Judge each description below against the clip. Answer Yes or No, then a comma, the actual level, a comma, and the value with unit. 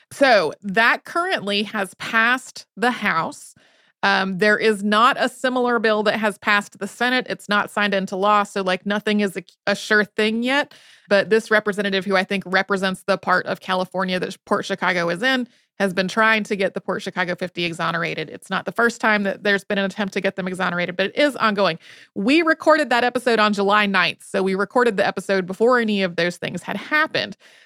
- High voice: Yes, high, 205 Hz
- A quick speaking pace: Yes, fast, 210 wpm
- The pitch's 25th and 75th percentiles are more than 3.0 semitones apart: No, narrow, 2.6 semitones